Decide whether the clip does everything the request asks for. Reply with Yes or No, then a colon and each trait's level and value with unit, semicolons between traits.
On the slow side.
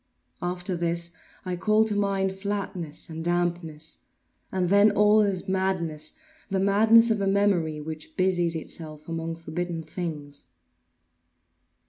Yes: slow, 120 wpm